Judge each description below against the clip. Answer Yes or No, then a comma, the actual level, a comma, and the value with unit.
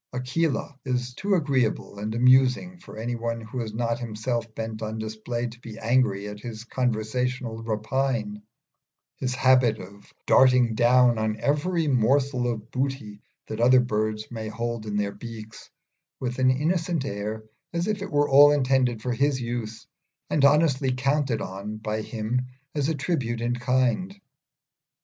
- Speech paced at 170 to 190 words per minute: No, average, 155 wpm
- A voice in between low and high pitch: No, low, 120 Hz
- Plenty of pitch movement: No, average, 3.4 semitones